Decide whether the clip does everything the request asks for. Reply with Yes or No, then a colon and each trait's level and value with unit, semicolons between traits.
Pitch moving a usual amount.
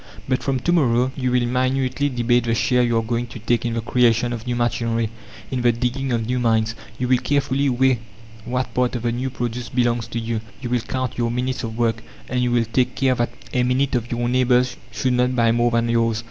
No: narrow, 1.4 semitones